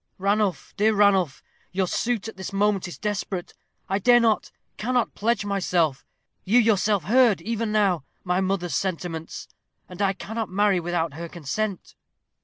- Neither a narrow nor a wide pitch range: Yes, average, 3.2 semitones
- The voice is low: No, high, 195 Hz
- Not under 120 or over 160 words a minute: Yes, average, 150 wpm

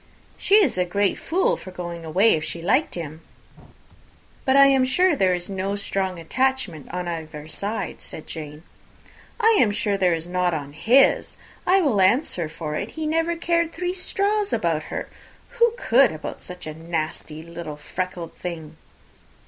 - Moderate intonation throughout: No, wide, 8.4 semitones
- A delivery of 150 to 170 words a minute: Yes, average, 165 wpm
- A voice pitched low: No, medium, 185 Hz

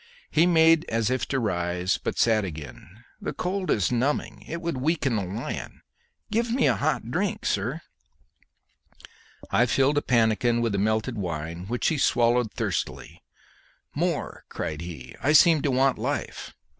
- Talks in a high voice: No, low, 120 Hz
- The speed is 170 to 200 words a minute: No, average, 155 wpm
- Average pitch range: No, wide, 6.8 semitones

